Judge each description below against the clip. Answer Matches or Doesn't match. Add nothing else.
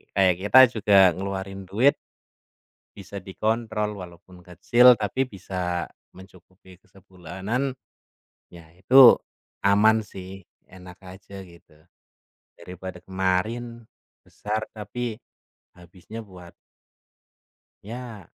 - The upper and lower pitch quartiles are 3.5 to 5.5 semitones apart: Doesn't match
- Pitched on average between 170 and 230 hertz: Doesn't match